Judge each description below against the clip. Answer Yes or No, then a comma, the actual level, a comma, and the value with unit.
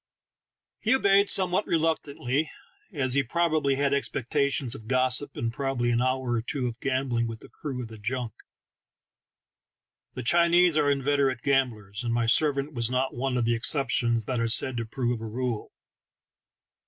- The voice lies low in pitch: Yes, low, 130 Hz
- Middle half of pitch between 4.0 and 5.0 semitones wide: No, average, 3.3 semitones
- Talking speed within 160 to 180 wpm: Yes, average, 170 wpm